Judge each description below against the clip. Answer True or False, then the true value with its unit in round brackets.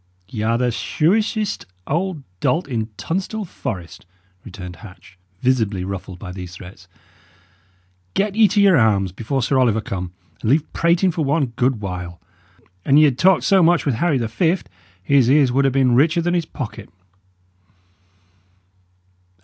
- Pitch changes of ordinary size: False (8.7 semitones)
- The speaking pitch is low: True (130 Hz)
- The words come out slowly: False (155 wpm)